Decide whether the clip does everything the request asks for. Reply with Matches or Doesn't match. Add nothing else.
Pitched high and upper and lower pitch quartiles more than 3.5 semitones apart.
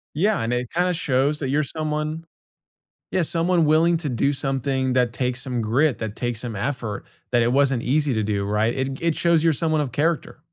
Doesn't match